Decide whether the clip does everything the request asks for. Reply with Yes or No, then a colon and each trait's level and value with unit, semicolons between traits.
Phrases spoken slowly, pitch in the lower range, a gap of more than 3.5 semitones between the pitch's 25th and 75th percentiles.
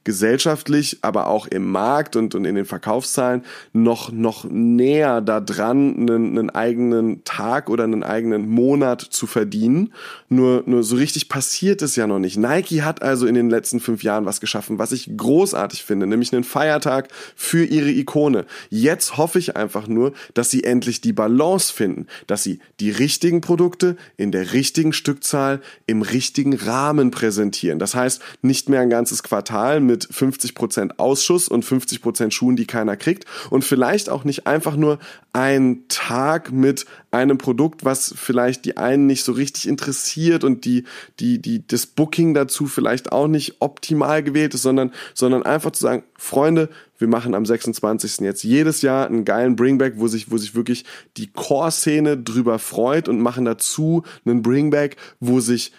No: average, 170 wpm; low, 130 Hz; average, 4.1 semitones